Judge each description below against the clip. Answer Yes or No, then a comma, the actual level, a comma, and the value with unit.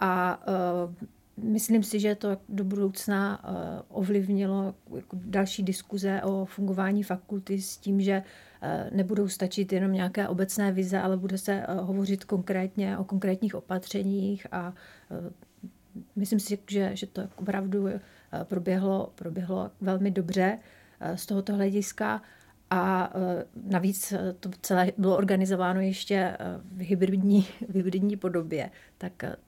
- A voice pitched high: Yes, high, 195 Hz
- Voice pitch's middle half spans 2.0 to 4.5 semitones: No, narrow, 1.1 semitones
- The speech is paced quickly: No, average, 140 wpm